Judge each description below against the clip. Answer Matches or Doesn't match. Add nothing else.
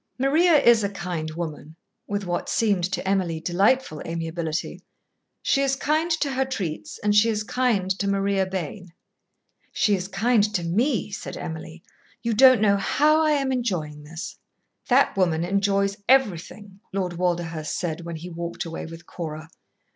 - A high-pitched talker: Matches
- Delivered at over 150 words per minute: Matches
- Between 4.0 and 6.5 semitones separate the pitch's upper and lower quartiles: Matches